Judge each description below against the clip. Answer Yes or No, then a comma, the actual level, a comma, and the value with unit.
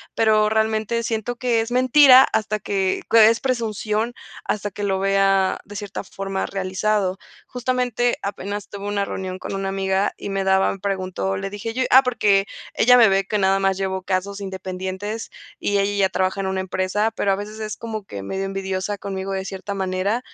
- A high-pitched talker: Yes, high, 200 Hz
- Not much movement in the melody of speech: Yes, narrow, 2.2 semitones